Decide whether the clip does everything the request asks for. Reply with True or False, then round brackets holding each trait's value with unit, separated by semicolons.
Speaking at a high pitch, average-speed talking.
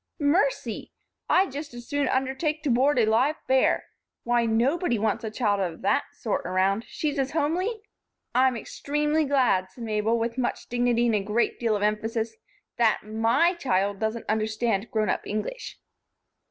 True (235 Hz; 165 wpm)